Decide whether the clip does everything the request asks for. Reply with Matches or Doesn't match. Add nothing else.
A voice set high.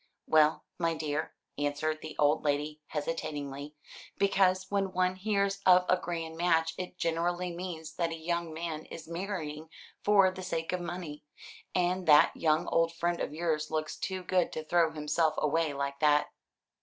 Doesn't match